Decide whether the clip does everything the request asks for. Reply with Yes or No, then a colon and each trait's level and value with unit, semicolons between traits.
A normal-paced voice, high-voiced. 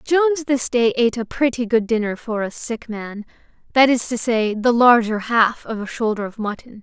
No: fast, 210 wpm; high, 235 Hz